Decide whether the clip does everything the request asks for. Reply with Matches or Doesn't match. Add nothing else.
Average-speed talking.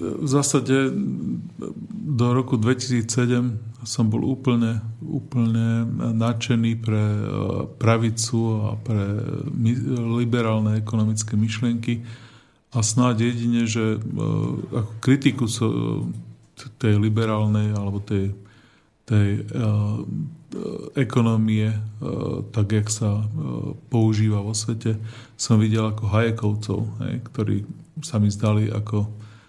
Doesn't match